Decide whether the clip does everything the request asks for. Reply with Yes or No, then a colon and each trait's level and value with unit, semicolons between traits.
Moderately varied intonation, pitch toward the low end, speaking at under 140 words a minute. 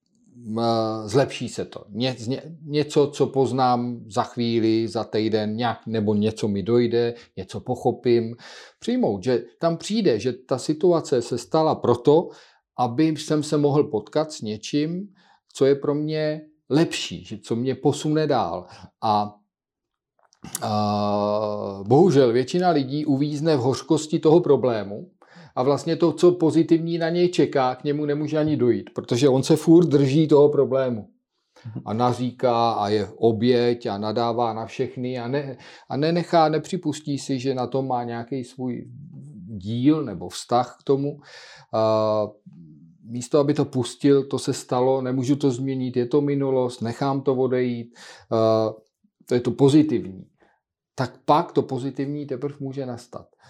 No: average, 4.1 semitones; low, 130 Hz; average, 145 wpm